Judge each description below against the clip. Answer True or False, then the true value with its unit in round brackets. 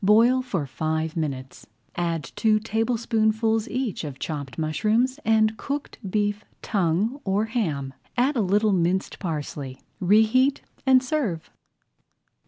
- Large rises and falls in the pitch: True (6.0 semitones)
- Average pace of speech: False (120 wpm)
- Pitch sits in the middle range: False (210 Hz)